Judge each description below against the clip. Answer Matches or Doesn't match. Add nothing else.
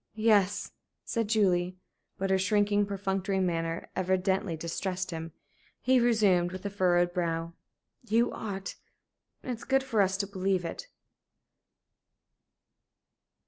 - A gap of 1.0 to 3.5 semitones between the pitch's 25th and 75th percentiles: Matches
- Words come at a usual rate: Doesn't match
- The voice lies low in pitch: Doesn't match